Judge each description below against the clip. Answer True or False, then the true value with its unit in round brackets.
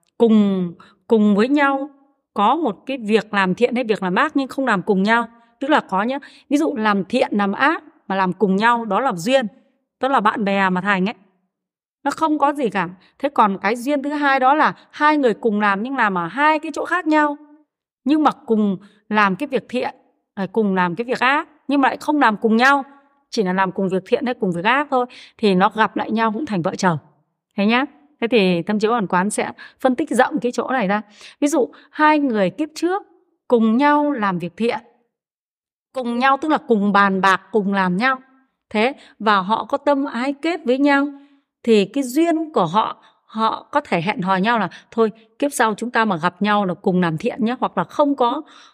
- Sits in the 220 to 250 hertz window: True (240 Hz)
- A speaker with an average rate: True (225 wpm)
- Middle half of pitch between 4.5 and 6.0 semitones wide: True (5.5 semitones)